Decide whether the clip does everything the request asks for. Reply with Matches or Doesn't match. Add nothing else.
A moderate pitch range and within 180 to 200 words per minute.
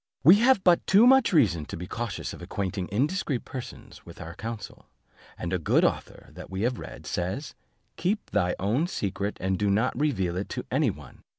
Doesn't match